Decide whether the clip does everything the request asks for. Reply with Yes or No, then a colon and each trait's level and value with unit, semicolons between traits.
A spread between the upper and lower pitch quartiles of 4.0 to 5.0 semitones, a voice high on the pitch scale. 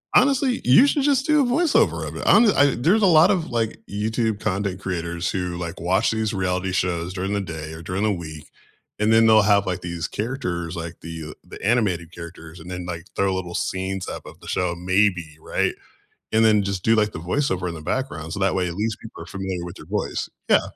No: average, 4.5 semitones; very low, 95 Hz